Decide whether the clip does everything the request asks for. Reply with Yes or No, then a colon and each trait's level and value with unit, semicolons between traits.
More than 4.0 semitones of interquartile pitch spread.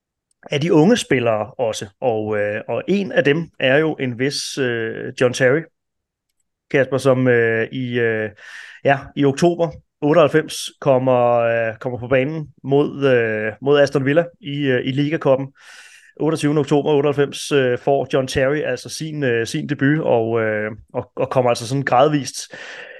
No: average, 3.5 semitones